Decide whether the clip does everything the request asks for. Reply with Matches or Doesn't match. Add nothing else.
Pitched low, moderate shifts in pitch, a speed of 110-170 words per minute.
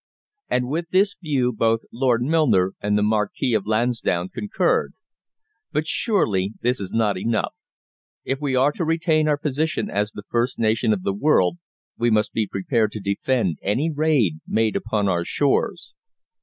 Doesn't match